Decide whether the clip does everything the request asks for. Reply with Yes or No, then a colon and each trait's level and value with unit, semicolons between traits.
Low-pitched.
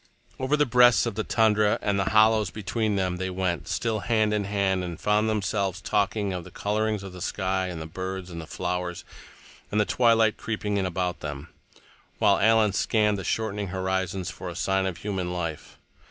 Yes: low, 100 Hz